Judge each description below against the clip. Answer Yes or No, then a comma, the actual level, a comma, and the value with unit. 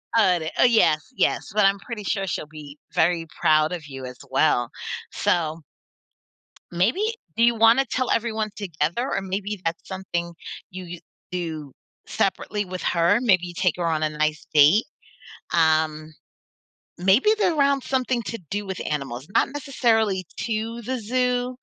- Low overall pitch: No, medium, 185 Hz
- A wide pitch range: Yes, wide, 6.3 semitones